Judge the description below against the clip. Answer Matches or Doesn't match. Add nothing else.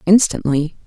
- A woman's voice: Matches